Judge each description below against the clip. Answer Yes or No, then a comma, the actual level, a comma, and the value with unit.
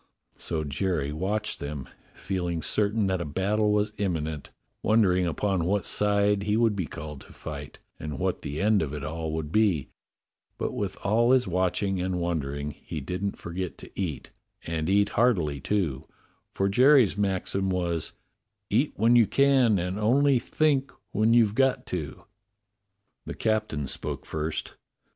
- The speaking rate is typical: Yes, average, 155 wpm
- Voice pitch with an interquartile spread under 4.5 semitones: No, average, 5.0 semitones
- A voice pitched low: Yes, very low, 95 Hz